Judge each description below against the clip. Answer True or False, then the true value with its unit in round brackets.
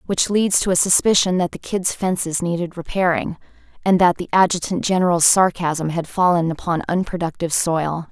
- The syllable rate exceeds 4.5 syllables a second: True (5.3 syllables/s)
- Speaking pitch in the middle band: True (175 Hz)